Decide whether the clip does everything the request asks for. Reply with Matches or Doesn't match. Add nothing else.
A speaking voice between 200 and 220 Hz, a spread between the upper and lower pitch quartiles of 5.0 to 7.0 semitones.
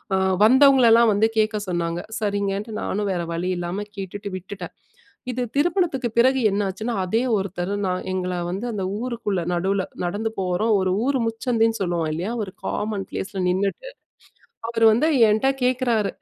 Doesn't match